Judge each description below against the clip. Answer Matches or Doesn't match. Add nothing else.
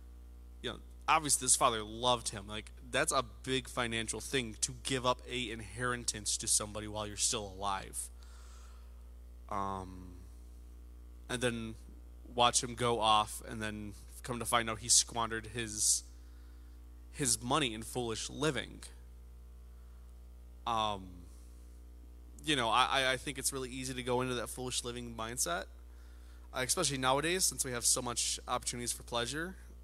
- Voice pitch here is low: Matches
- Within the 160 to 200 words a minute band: Doesn't match